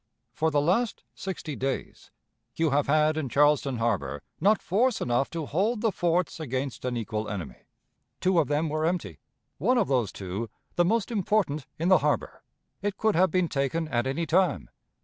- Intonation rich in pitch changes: Yes, wide, 5.9 semitones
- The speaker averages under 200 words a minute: Yes, average, 180 wpm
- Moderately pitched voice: Yes, medium, 155 Hz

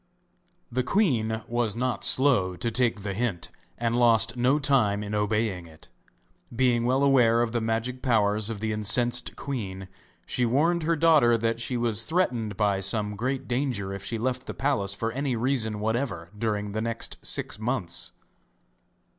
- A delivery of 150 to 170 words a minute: Yes, average, 165 wpm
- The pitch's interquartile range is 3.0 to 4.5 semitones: Yes, average, 3.3 semitones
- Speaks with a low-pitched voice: Yes, low, 115 Hz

